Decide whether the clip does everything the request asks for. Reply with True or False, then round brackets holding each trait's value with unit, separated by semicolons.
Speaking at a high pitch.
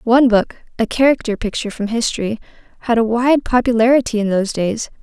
True (230 Hz)